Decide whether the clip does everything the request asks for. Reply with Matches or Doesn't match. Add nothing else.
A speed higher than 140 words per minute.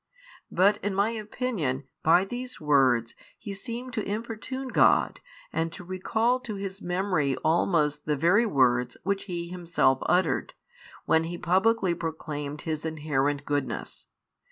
Doesn't match